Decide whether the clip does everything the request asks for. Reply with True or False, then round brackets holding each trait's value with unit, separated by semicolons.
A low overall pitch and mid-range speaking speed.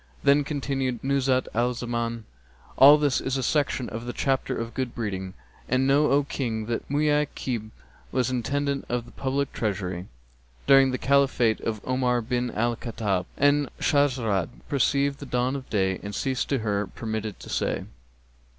True (125 Hz; 160 wpm)